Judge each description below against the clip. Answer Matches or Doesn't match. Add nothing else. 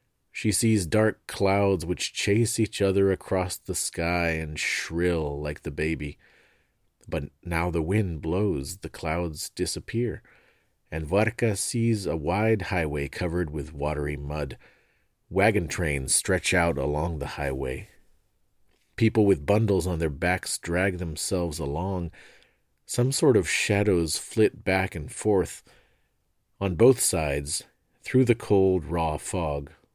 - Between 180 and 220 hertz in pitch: Doesn't match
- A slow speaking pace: Matches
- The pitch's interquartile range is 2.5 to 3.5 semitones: Doesn't match